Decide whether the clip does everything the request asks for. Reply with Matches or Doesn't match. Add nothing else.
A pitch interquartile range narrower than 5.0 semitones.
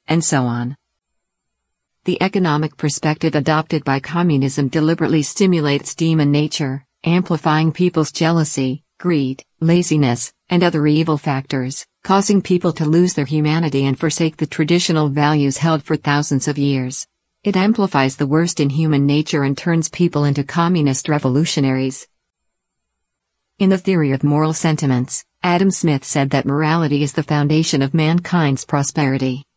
Matches